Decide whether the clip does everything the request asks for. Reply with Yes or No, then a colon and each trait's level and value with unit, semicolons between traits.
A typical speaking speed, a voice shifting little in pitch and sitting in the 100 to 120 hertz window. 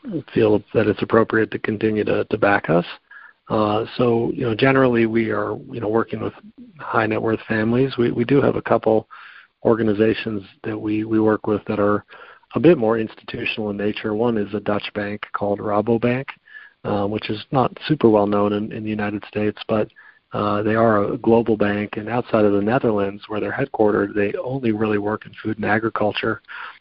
Yes: average, 195 wpm; narrow, 1.9 semitones; low, 110 Hz